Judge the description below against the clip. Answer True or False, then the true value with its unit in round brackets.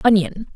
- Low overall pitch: False (200 Hz)